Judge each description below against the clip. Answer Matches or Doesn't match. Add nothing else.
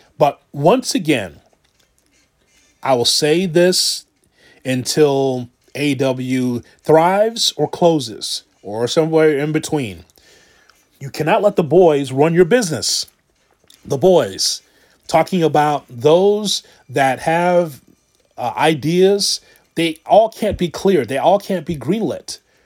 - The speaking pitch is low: Doesn't match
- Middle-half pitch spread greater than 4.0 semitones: Matches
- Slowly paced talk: Matches